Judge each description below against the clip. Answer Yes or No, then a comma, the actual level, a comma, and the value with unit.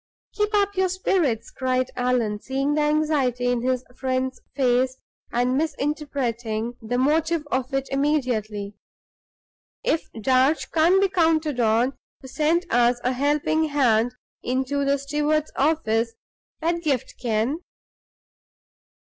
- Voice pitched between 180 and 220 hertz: No, very high, 265 Hz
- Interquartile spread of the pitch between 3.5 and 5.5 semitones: Yes, average, 3.8 semitones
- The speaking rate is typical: No, slow, 120 wpm